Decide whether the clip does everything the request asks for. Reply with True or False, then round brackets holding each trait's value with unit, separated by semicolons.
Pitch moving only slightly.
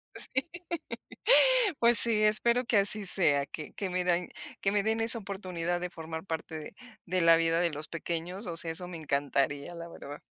False (3.7 semitones)